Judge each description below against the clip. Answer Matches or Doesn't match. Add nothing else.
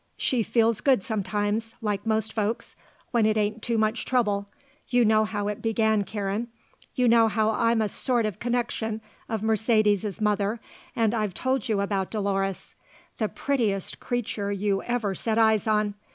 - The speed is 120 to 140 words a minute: Doesn't match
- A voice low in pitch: Doesn't match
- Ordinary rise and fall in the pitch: Doesn't match